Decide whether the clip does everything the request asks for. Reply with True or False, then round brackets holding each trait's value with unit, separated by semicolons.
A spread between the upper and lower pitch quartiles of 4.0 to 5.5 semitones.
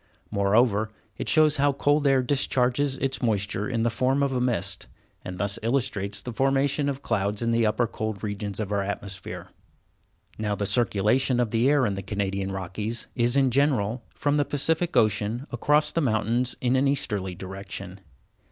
True (4.9 semitones)